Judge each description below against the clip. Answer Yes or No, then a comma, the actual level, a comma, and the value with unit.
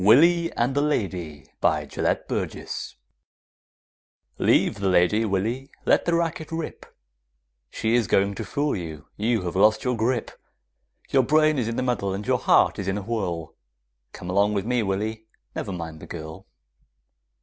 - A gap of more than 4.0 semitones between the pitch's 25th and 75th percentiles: Yes, average, 5.0 semitones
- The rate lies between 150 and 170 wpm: Yes, average, 165 wpm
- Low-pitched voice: Yes, low, 110 Hz